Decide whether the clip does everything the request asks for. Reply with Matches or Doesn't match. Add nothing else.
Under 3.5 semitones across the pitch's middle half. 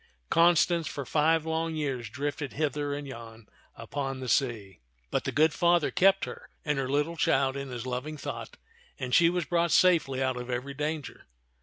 Doesn't match